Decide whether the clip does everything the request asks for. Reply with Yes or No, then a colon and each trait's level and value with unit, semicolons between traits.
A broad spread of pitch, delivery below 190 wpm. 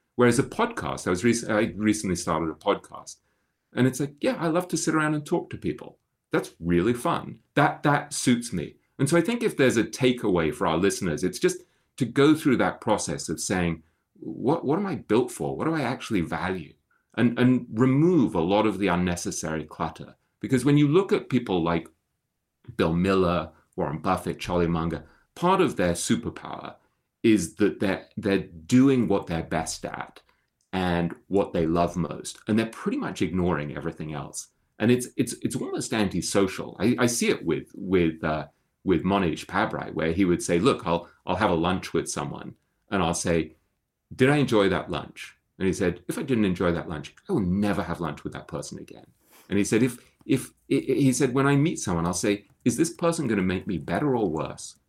No: wide, 7.4 semitones; fast, 205 wpm